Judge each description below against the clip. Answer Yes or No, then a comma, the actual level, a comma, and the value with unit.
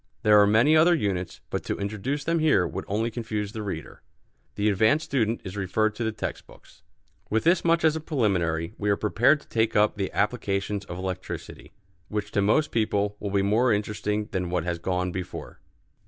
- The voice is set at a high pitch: No, low, 105 Hz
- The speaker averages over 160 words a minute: Yes, average, 200 wpm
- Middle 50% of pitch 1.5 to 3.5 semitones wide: Yes, average, 2.9 semitones